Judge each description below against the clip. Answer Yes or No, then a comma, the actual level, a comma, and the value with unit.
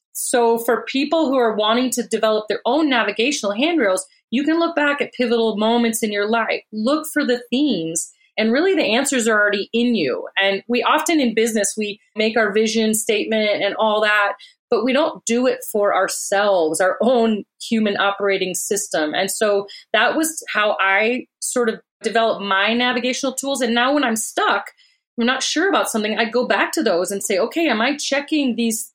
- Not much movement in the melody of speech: No, average, 4.3 semitones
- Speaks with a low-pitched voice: No, high, 230 Hz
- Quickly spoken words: No, average, 195 wpm